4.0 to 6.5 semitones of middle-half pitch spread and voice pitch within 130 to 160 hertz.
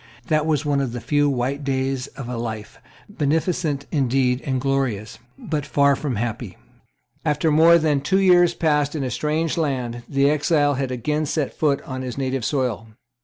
No: average, 3.1 semitones; medium, 140 Hz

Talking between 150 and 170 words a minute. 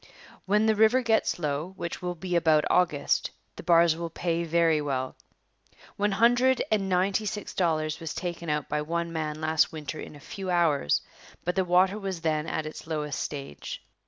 No: average, 185 wpm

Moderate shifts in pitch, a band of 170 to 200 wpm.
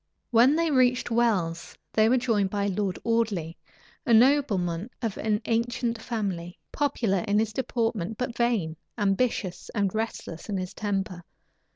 No: average, 3.7 semitones; average, 145 wpm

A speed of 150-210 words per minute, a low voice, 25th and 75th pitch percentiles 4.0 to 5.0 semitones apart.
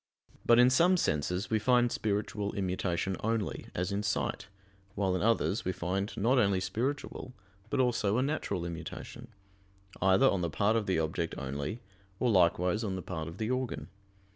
Yes: average, 170 wpm; low, 100 Hz; average, 4.6 semitones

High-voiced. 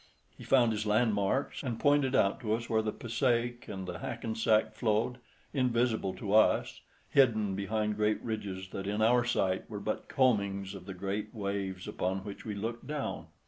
No: low, 110 Hz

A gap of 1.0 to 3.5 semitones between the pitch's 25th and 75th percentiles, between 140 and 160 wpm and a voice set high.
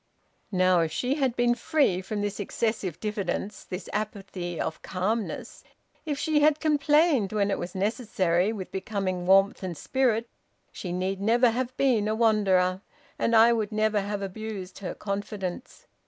No: average, 3.9 semitones; average, 155 wpm; high, 210 Hz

